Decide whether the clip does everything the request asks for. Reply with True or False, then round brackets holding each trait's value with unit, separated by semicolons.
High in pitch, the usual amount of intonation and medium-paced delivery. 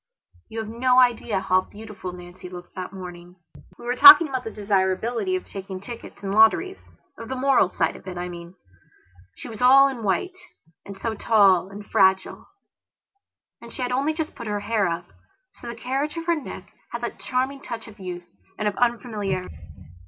True (220 Hz; 4.9 semitones; 190 wpm)